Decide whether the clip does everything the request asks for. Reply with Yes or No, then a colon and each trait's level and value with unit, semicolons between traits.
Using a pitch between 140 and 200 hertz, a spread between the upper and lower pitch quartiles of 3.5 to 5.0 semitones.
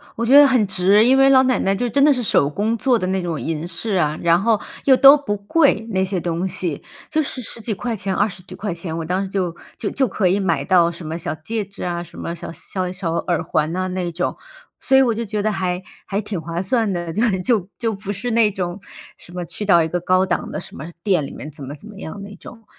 Yes: high, 190 Hz; average, 4.4 semitones